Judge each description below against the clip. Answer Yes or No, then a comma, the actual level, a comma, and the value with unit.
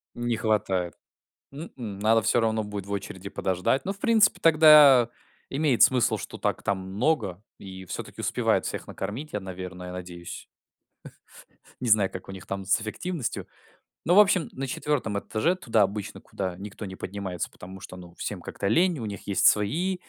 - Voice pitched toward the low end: Yes, low, 105 Hz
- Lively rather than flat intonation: Yes, wide, 6.3 semitones